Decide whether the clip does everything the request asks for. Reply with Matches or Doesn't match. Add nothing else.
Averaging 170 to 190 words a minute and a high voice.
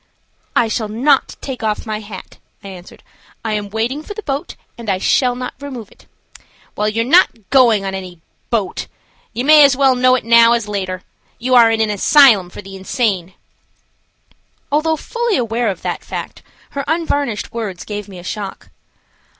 Matches